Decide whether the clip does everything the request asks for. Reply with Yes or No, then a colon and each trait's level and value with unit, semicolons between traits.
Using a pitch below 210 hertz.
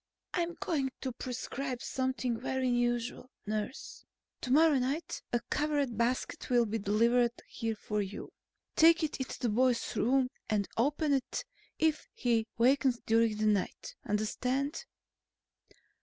No: very high, 250 Hz